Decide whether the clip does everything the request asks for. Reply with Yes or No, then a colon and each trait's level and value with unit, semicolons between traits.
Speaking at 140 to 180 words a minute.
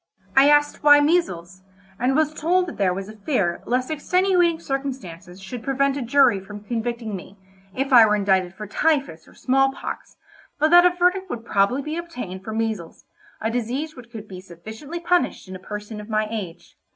No: average, 190 wpm